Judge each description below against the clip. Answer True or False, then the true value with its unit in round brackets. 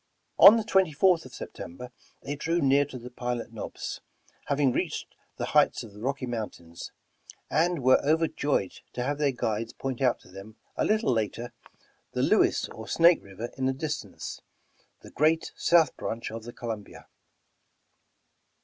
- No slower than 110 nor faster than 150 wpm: False (160 wpm)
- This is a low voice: True (130 Hz)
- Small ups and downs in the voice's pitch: False (5.0 semitones)